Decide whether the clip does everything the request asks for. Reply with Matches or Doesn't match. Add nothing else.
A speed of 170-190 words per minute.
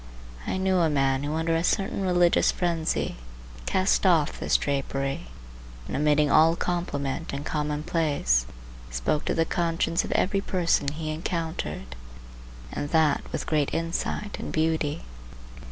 Doesn't match